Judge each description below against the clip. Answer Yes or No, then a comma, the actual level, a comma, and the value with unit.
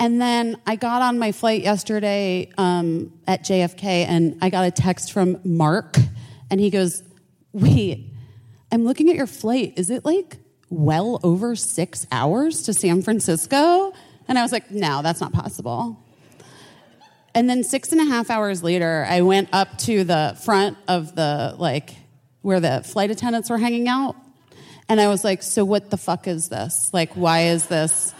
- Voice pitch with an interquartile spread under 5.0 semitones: No, average, 5.3 semitones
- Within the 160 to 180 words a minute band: Yes, average, 175 wpm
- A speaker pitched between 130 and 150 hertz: No, high, 190 Hz